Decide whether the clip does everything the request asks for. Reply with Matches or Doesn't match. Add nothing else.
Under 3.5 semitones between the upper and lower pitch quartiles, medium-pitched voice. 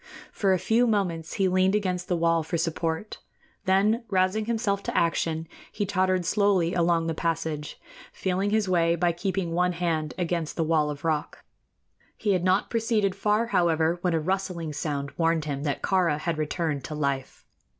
Matches